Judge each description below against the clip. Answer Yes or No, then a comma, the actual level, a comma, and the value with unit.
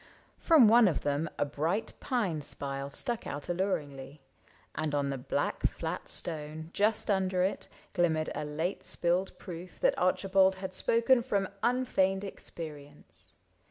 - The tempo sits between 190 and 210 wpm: No, average, 140 wpm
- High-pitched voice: No, medium, 175 Hz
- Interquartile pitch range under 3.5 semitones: No, average, 5.2 semitones